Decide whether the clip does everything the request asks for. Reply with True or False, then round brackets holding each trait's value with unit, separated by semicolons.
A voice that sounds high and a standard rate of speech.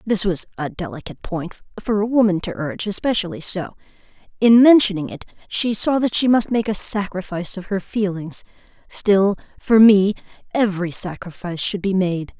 True (195 Hz; 160 wpm)